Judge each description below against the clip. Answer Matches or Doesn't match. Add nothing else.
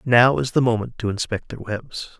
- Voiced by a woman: Doesn't match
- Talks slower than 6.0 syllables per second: Matches